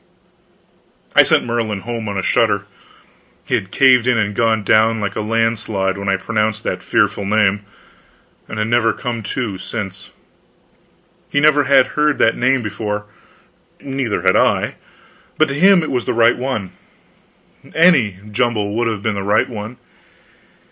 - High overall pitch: No, low, 110 Hz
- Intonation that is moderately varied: Yes, average, 3.1 semitones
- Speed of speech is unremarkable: Yes, average, 160 wpm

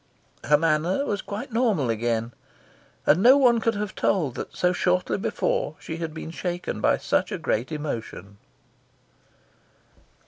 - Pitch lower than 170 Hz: No, medium, 175 Hz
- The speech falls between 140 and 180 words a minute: Yes, average, 145 wpm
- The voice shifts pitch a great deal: Yes, wide, 6.2 semitones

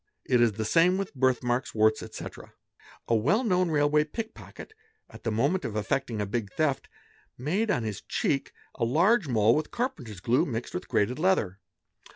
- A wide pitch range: Yes, wide, 7.9 semitones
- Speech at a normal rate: Yes, average, 180 wpm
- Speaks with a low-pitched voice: Yes, low, 130 Hz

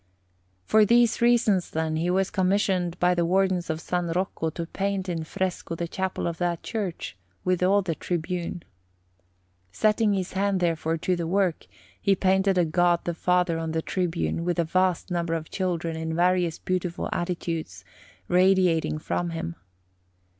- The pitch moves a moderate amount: No, narrow, 2.2 semitones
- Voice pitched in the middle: Yes, medium, 175 Hz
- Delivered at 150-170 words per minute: Yes, average, 160 wpm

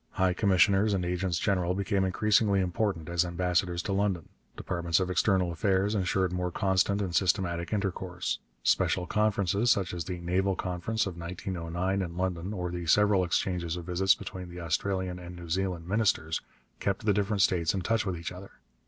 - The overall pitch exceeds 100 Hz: No, very low, 90 Hz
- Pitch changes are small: Yes, narrow, 2.1 semitones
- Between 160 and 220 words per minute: Yes, average, 180 wpm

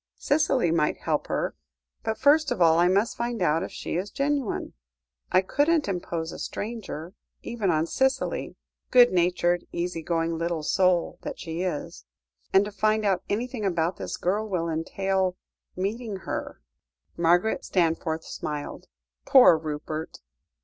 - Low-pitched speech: No, medium, 185 Hz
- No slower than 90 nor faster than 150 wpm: Yes, average, 145 wpm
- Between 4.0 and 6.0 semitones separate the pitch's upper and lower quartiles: Yes, average, 4.8 semitones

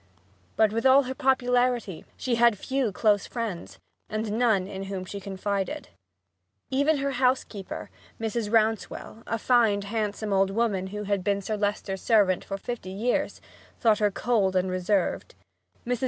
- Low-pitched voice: No, high, 215 Hz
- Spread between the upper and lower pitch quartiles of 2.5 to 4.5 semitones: Yes, average, 3.4 semitones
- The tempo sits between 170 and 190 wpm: No, average, 155 wpm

